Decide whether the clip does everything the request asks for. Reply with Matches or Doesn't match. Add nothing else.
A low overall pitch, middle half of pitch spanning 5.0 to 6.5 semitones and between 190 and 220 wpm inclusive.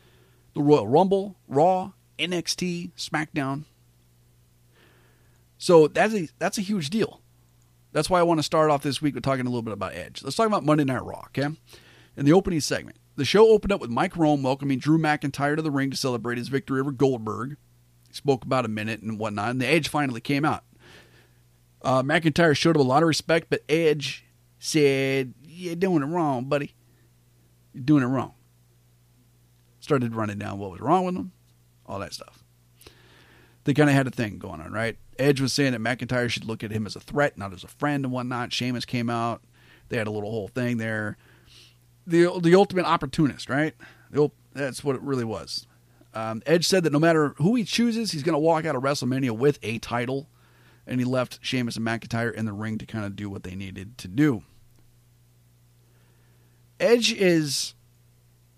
Matches